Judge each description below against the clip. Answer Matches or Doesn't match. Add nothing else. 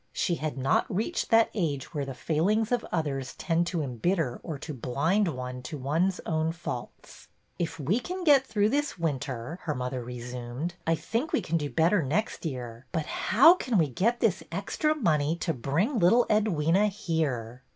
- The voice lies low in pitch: Doesn't match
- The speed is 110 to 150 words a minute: Doesn't match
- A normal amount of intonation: Doesn't match